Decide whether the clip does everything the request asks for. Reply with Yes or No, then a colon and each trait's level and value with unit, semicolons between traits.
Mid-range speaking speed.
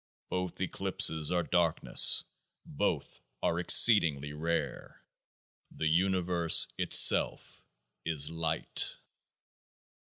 No: slow, 85 wpm